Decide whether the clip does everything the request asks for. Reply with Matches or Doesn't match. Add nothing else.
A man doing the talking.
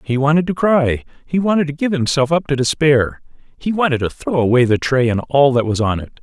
Matches